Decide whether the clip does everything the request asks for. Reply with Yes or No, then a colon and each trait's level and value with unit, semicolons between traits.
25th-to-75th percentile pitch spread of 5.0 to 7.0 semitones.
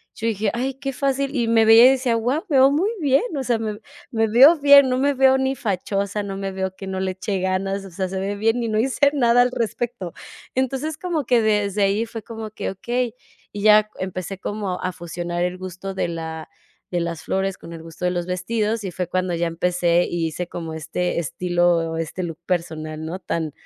Yes: average, 5.3 semitones